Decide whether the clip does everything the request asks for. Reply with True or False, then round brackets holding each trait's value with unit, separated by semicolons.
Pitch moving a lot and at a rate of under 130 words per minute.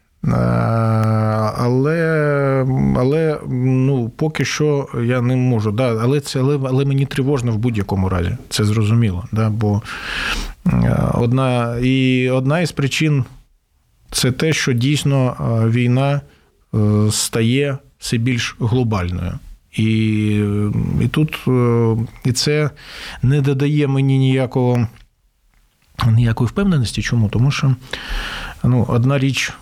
False (3.6 semitones; 105 wpm)